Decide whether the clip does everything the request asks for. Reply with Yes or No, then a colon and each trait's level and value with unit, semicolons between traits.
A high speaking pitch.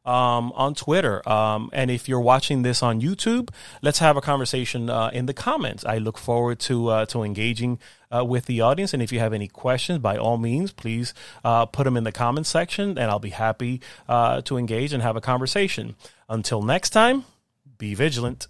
No: low, 125 Hz